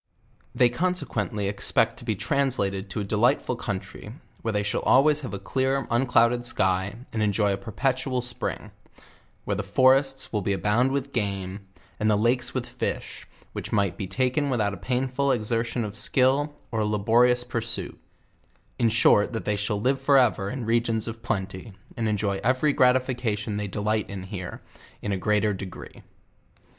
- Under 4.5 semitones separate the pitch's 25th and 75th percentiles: Yes, average, 3.8 semitones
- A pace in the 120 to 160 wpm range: No, average, 170 wpm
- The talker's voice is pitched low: Yes, low, 115 Hz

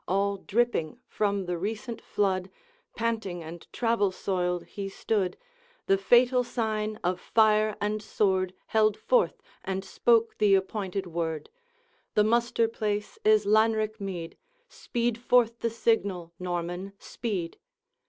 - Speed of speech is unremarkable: No, slow, 125 wpm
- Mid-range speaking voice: No, high, 205 Hz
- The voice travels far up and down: No, average, 3.2 semitones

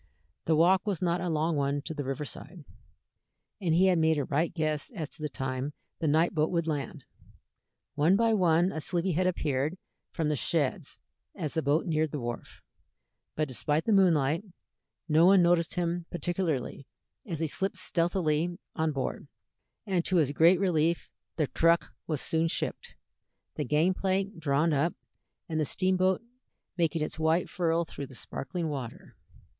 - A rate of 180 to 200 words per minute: No, average, 170 wpm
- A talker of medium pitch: Yes, medium, 160 Hz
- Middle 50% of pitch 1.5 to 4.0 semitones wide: Yes, average, 2.8 semitones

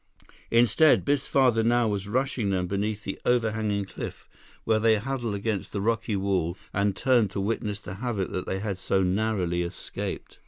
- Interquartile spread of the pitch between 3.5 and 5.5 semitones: No, average, 3.0 semitones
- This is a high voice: No, low, 105 Hz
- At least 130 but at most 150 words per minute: No, average, 170 wpm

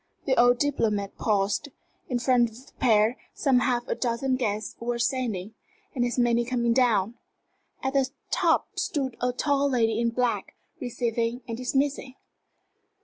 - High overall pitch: Yes, high, 245 Hz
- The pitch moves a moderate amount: No, narrow, 2.0 semitones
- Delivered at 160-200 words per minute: No, average, 150 wpm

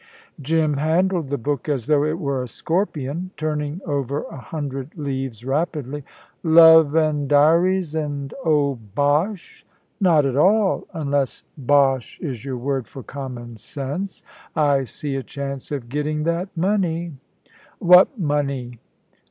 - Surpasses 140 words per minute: No, slow, 135 wpm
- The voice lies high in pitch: No, medium, 145 Hz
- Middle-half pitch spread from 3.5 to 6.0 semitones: No, average, 3.0 semitones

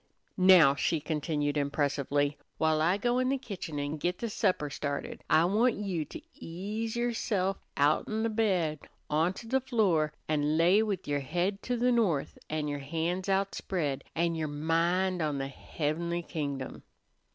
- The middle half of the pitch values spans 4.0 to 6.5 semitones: Yes, average, 5.1 semitones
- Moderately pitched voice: Yes, medium, 165 Hz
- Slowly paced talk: No, average, 165 wpm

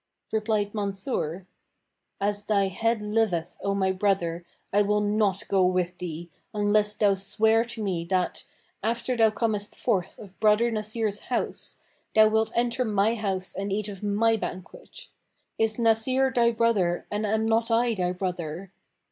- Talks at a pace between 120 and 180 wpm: Yes, average, 155 wpm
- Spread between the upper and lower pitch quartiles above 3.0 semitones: No, narrow, 2.6 semitones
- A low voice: No, high, 210 Hz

